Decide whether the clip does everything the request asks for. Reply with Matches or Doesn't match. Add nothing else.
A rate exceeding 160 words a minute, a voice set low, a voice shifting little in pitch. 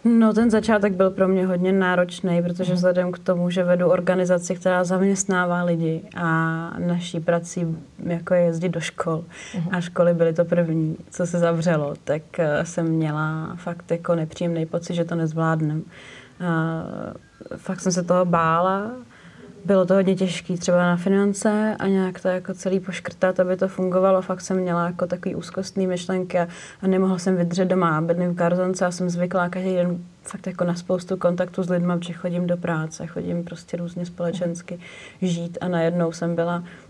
Doesn't match